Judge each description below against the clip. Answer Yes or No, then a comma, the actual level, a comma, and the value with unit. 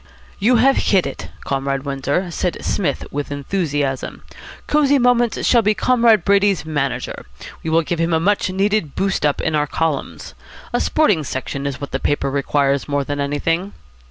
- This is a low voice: No, medium, 160 Hz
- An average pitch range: No, wide, 6.2 semitones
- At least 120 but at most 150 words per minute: No, average, 170 wpm